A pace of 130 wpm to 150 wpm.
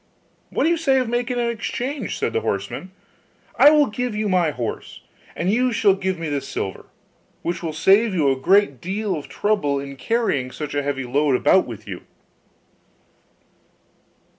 No: average, 175 wpm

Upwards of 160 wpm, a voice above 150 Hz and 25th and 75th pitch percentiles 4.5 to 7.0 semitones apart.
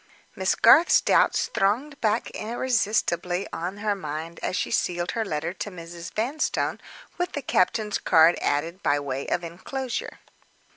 No: average, 145 wpm; medium, 185 Hz; average, 4.9 semitones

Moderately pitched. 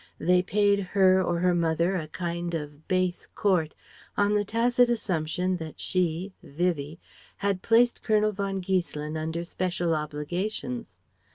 Yes: medium, 180 Hz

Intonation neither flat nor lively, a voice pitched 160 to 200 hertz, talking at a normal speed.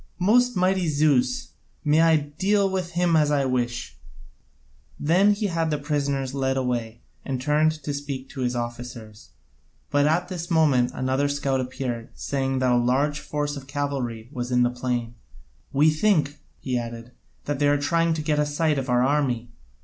No: average, 3.9 semitones; medium, 145 Hz; average, 175 wpm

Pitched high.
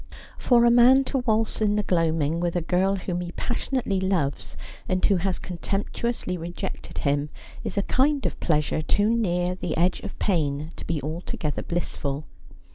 No: medium, 180 Hz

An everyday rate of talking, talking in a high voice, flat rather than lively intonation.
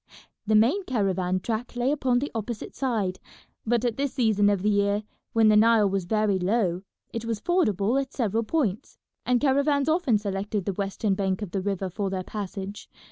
No: average, 190 wpm; high, 215 Hz; average, 3.7 semitones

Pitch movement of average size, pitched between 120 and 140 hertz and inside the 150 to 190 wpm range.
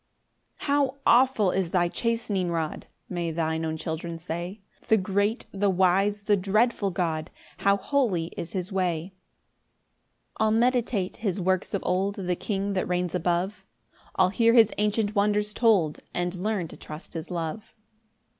No: average, 3.3 semitones; high, 190 Hz; average, 155 wpm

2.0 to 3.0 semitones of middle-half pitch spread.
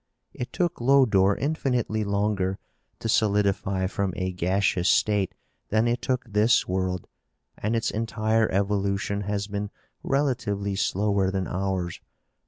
Yes: narrow, 2.5 semitones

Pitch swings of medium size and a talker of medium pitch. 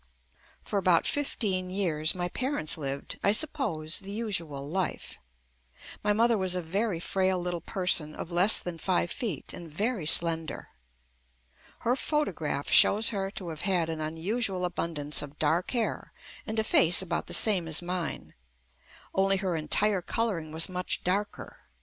Yes: average, 3.9 semitones; medium, 180 Hz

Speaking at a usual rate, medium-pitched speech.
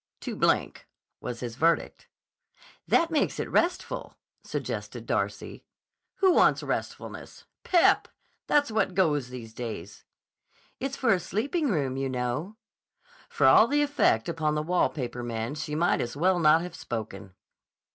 Yes: average, 145 wpm; medium, 155 Hz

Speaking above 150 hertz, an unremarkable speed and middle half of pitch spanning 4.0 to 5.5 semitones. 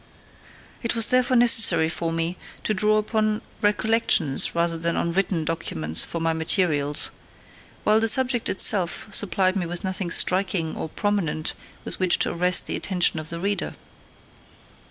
Yes: medium, 185 Hz; average, 155 wpm; average, 4.3 semitones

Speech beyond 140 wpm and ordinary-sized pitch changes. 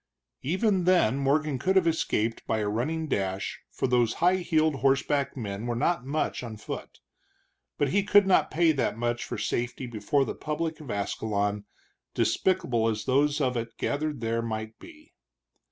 No: average, 170 wpm; wide, 5.8 semitones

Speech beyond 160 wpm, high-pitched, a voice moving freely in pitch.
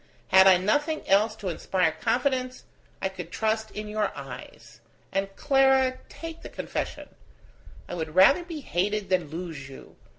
No: average, 155 wpm; high, 210 Hz; wide, 6.0 semitones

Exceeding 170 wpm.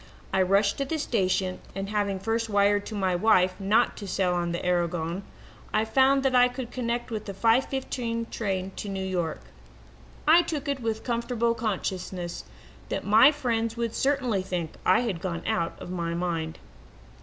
Yes: average, 180 wpm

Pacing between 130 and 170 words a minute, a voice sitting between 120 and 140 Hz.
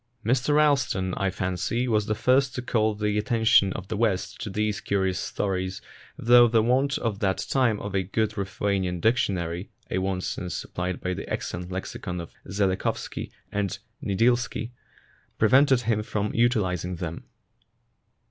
No: average, 155 wpm; low, 105 Hz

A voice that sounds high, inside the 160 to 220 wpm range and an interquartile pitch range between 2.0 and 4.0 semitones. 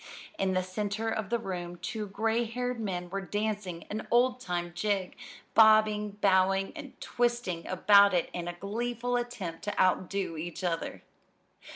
No: high, 200 Hz; average, 150 wpm; average, 3.5 semitones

